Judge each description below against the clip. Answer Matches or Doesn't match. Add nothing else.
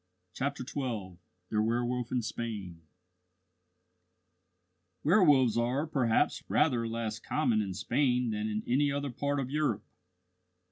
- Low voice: Matches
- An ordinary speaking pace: Doesn't match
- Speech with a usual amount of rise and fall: Matches